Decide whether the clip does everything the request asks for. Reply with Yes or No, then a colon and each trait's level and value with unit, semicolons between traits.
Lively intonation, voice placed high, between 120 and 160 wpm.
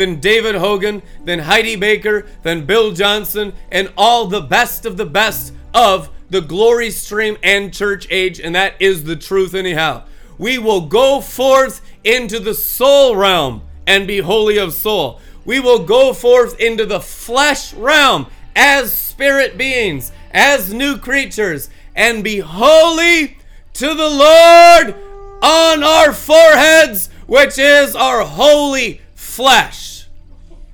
Yes: wide, 6.5 semitones; high, 220 Hz; slow, 135 wpm